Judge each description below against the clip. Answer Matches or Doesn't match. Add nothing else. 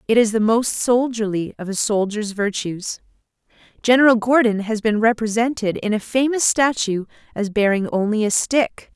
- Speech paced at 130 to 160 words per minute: Matches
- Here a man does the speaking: Doesn't match